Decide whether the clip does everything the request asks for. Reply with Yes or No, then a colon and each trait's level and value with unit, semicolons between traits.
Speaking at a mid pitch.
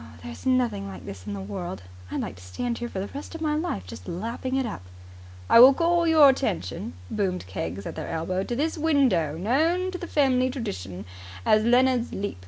No: high, 235 Hz